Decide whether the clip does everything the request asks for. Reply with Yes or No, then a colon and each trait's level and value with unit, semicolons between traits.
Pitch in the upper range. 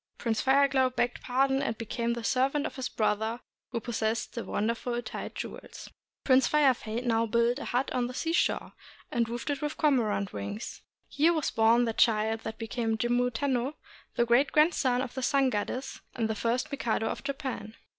Yes: high, 245 Hz